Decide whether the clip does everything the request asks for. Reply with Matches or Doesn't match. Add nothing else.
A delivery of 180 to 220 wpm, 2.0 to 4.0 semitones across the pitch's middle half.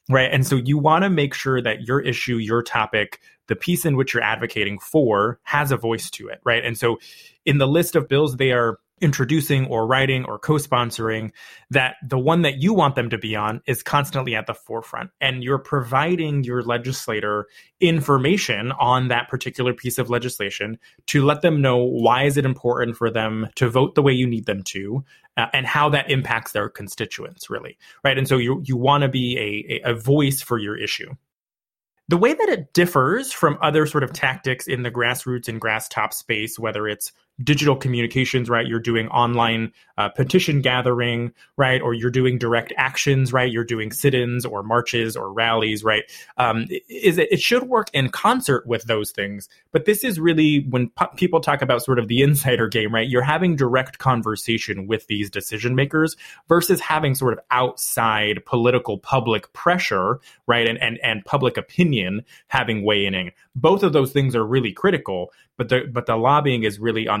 Matches